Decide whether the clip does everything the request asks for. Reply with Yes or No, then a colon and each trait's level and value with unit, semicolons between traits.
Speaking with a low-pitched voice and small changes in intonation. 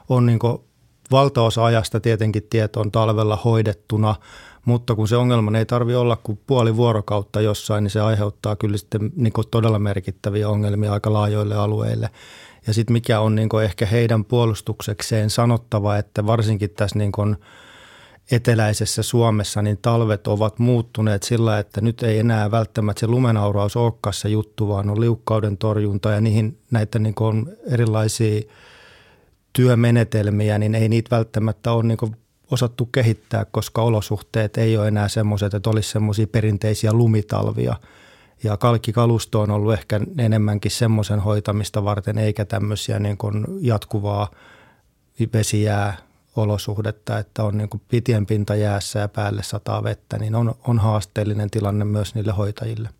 Yes: low, 110 Hz; narrow, 1.6 semitones